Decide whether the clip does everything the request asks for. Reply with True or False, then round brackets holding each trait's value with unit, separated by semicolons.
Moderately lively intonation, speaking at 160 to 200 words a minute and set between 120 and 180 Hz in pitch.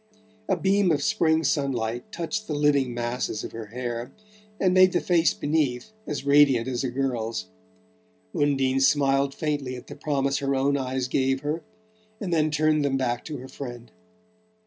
True (3.3 semitones; 170 wpm; 140 Hz)